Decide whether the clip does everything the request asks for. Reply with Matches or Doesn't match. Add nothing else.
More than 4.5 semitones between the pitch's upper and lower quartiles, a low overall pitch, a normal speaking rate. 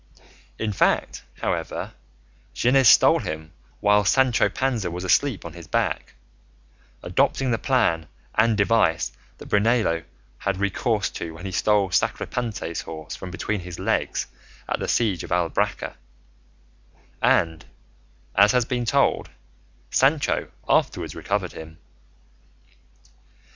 Doesn't match